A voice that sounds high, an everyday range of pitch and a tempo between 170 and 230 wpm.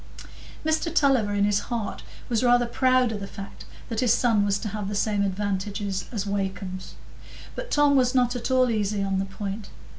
Yes: high, 210 Hz; average, 3.7 semitones; average, 190 wpm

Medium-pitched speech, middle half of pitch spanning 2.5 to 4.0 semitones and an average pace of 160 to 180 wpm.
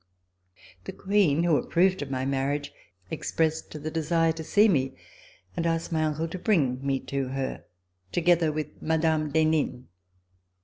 No: medium, 155 Hz; average, 3.0 semitones; average, 150 wpm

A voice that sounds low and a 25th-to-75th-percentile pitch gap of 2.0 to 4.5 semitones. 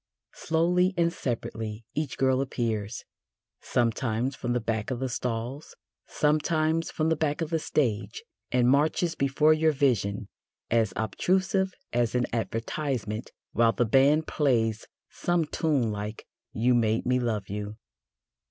No: low, 125 Hz; wide, 5.4 semitones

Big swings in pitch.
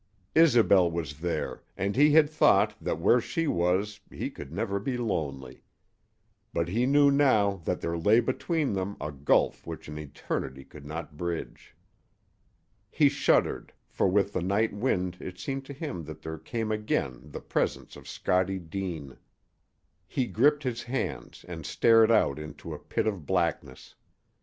Yes: wide, 6.9 semitones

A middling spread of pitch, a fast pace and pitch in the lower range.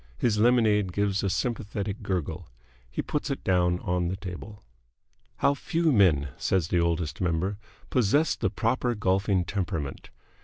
No: average, 3.5 semitones; average, 145 wpm; very low, 95 Hz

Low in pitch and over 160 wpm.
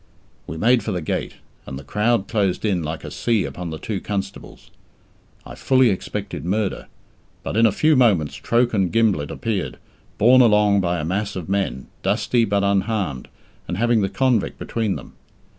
Yes: low, 100 Hz; average, 175 wpm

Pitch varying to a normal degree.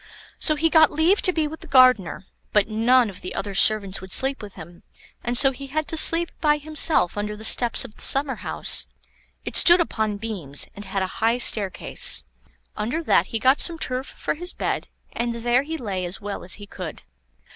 No: wide, 6.5 semitones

